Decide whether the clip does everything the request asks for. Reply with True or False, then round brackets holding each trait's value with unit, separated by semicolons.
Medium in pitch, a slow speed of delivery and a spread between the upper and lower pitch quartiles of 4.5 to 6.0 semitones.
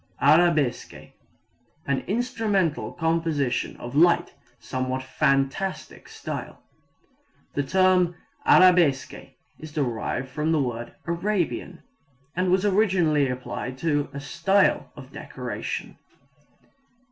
True (160 Hz; 95 wpm; 5.2 semitones)